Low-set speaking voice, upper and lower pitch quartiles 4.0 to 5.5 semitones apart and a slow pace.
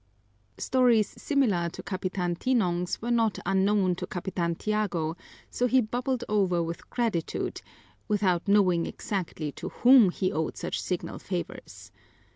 No: high, 195 Hz; average, 4.5 semitones; slow, 130 wpm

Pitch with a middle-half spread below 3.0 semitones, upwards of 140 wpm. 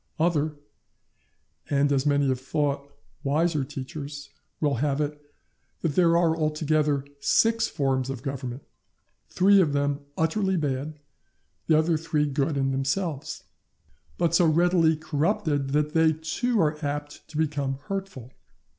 No: narrow, 2.5 semitones; slow, 135 wpm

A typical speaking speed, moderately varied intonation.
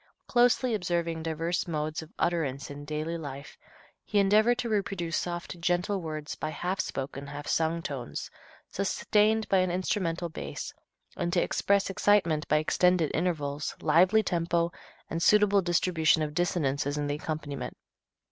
Yes: average, 145 wpm; average, 3.6 semitones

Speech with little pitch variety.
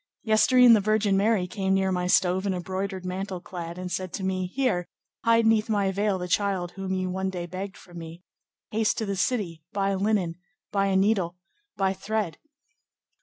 Yes: narrow, 2.2 semitones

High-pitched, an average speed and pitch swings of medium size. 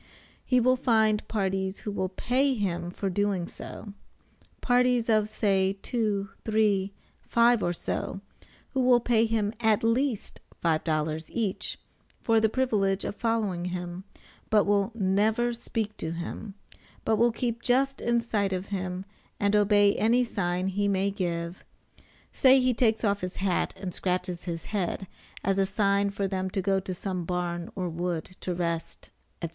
Yes: high, 200 Hz; average, 160 wpm; average, 3.5 semitones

